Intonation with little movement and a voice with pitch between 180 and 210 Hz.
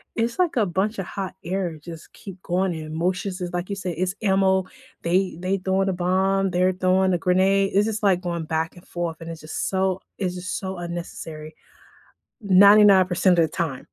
Yes: narrow, 1.9 semitones; medium, 185 Hz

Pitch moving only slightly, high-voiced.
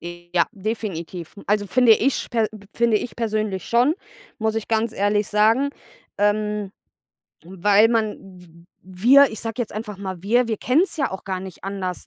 No: average, 3.1 semitones; high, 210 Hz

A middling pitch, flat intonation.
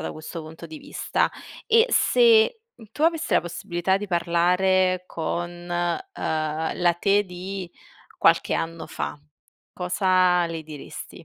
Yes: medium, 175 Hz; narrow, 2.3 semitones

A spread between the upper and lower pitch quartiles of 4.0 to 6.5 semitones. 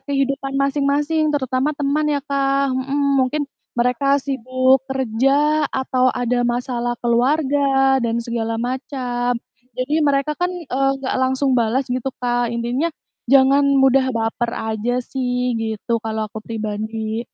No: narrow, 2.5 semitones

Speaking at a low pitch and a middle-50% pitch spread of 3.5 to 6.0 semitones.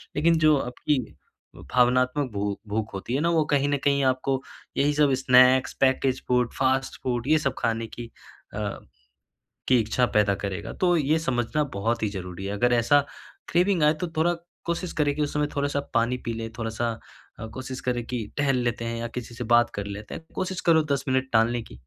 Yes: low, 130 Hz; average, 3.8 semitones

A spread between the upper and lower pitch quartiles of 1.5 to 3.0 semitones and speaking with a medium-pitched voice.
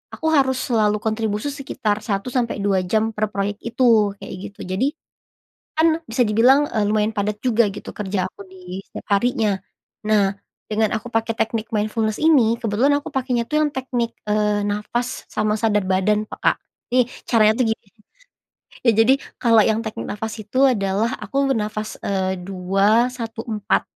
No: narrow, 2.6 semitones; high, 220 Hz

